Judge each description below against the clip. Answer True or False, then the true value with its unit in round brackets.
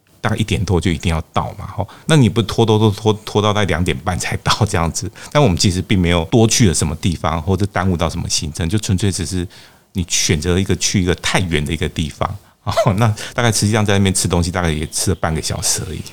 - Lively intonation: False (3.8 semitones)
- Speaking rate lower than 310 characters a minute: False (370 characters per minute)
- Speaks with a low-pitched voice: True (95 Hz)